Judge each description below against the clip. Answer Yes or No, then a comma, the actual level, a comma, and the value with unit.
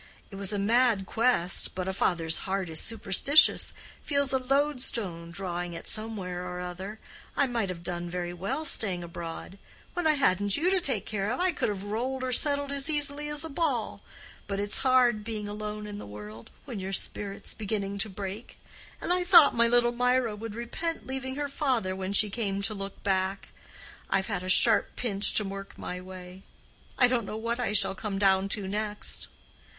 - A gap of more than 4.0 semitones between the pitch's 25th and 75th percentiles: Yes, average, 4.9 semitones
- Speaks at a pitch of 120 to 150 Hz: No, high, 210 Hz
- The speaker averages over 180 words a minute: Yes, average, 190 wpm